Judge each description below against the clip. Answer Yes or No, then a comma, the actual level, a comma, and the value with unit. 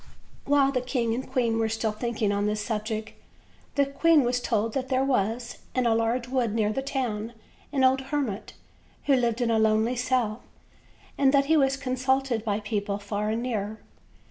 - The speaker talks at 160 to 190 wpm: Yes, average, 185 wpm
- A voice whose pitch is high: Yes, high, 235 Hz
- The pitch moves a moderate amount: Yes, average, 3.4 semitones